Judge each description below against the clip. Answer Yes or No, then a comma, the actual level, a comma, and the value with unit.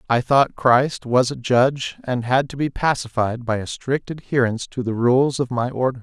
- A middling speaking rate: No, fast, 210 wpm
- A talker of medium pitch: No, low, 125 Hz